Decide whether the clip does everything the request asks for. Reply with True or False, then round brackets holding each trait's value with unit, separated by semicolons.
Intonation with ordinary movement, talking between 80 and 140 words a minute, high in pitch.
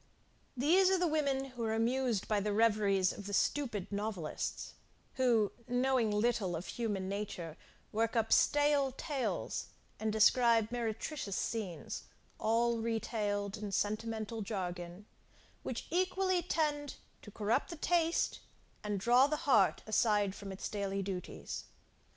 True (4.5 semitones; 135 wpm; 225 Hz)